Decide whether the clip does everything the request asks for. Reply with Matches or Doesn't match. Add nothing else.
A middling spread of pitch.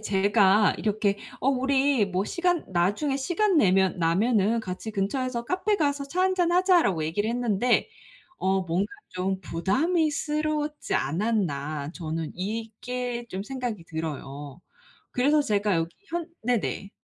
Doesn't match